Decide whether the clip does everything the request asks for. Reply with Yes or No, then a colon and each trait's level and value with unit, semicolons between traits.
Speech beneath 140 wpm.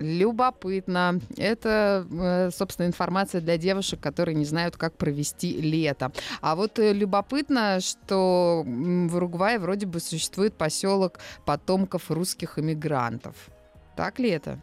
Yes: average, 115 wpm